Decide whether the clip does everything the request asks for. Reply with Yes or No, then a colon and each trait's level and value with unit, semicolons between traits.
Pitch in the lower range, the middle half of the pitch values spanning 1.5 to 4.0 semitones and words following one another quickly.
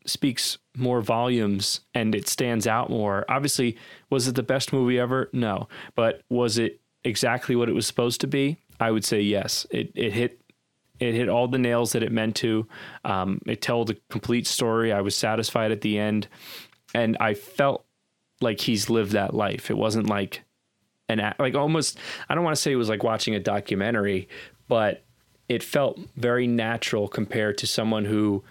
No: low, 115 Hz; narrow, 2.6 semitones; average, 185 wpm